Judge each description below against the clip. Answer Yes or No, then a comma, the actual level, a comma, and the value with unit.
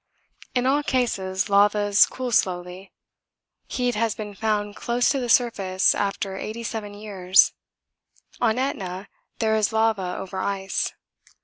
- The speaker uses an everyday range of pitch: Yes, average, 3.2 semitones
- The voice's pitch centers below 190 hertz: No, high, 210 Hz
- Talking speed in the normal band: No, slow, 125 wpm